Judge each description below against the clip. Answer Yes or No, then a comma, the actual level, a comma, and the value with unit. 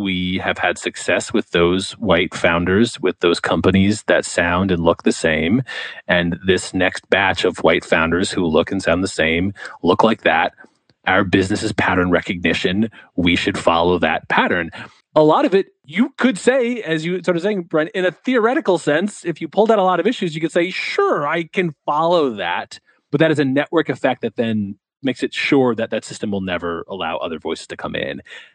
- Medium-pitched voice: Yes, medium, 145 Hz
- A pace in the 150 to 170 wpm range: No, fast, 205 wpm